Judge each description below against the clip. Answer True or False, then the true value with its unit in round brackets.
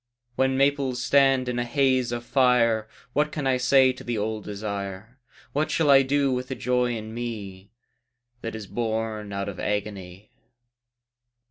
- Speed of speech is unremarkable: True (160 wpm)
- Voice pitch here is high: False (120 Hz)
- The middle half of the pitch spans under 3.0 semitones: False (3.7 semitones)